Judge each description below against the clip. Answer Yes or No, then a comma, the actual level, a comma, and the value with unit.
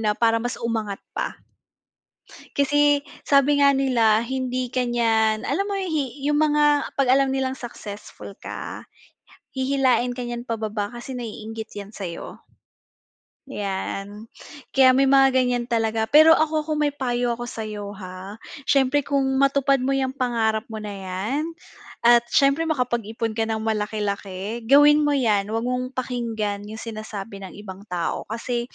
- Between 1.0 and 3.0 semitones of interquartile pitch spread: No, average, 3.9 semitones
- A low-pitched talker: No, high, 240 Hz